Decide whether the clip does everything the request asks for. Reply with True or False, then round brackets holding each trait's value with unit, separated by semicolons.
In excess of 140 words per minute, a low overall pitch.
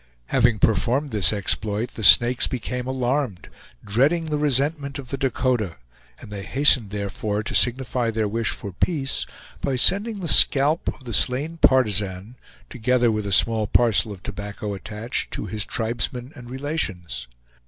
True (155 wpm; 120 Hz)